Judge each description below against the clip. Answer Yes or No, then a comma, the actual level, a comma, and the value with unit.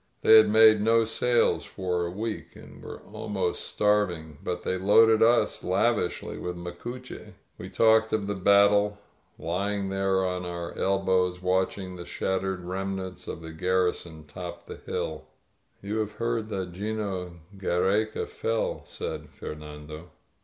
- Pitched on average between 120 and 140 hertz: No, very low, 95 Hz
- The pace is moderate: Yes, average, 145 wpm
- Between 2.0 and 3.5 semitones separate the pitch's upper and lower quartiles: Yes, average, 3.0 semitones